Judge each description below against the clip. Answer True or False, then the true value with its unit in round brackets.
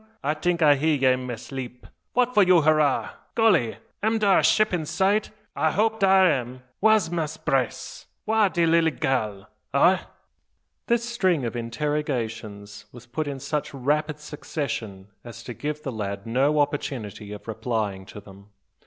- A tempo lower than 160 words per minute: False (165 wpm)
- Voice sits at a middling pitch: True (145 Hz)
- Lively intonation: True (6.5 semitones)